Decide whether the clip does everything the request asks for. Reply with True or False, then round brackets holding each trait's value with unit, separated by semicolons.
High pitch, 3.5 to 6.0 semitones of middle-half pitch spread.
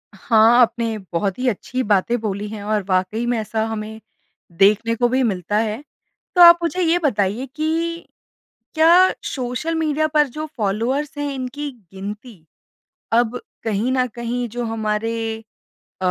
True (235 Hz; 4.8 semitones)